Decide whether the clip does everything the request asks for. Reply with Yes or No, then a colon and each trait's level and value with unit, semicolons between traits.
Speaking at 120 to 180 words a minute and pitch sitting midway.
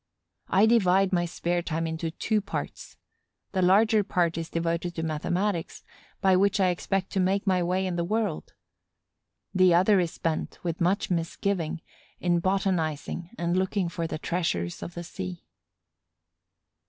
Yes: average, 155 wpm; medium, 180 Hz